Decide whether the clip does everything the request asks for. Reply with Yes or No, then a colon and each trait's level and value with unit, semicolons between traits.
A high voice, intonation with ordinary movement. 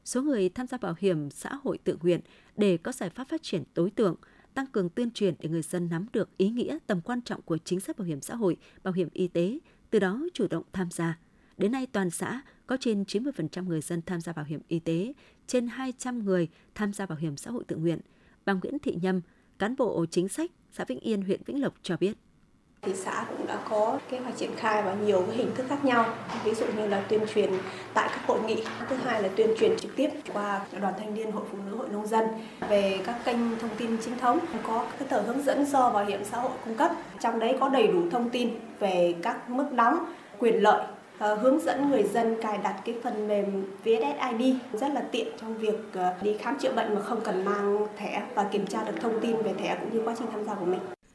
Yes: high, 215 Hz; average, 4.4 semitones